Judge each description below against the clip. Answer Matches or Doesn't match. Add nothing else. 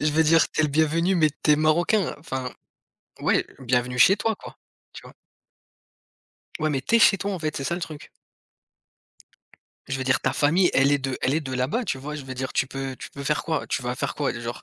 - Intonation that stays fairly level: Doesn't match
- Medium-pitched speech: Matches